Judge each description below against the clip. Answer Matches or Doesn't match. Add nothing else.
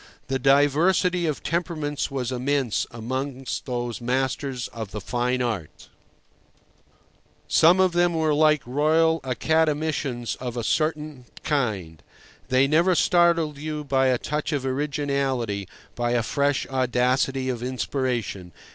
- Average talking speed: Doesn't match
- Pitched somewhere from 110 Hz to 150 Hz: Matches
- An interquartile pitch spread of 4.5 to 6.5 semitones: Doesn't match